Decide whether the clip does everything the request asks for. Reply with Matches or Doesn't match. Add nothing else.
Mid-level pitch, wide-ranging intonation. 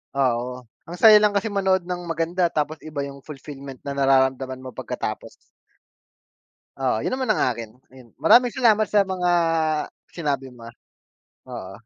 Matches